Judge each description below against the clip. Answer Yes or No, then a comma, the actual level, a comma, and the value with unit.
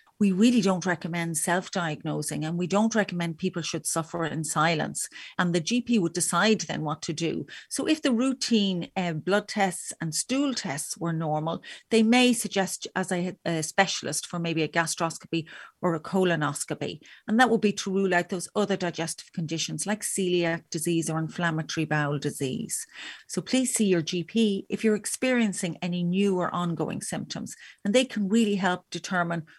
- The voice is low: No, medium, 180 Hz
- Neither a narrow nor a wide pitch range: Yes, average, 3.7 semitones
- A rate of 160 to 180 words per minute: Yes, average, 175 wpm